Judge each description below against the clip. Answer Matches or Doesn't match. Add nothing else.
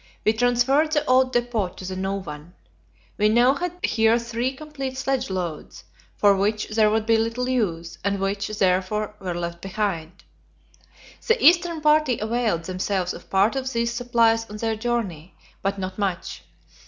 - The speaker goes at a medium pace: Matches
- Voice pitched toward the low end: Doesn't match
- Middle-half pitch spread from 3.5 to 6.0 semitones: Matches